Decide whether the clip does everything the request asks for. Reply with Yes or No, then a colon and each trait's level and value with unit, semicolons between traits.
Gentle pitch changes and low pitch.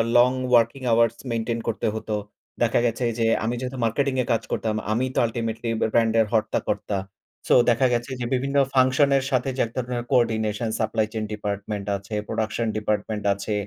Yes: narrow, 2.2 semitones; low, 115 Hz